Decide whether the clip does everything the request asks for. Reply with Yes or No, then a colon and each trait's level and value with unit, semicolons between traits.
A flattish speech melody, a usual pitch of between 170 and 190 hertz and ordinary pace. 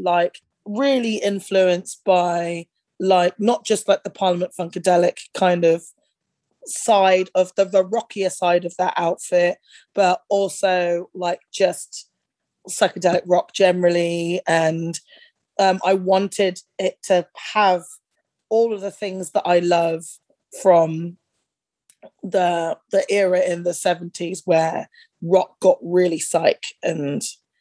No: narrow, 2.1 semitones; medium, 185 Hz; slow, 120 wpm